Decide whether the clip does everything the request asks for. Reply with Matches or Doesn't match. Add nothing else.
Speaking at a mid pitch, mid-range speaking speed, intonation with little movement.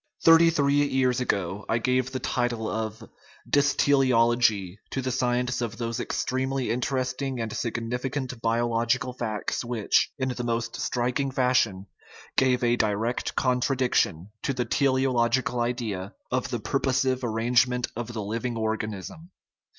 Doesn't match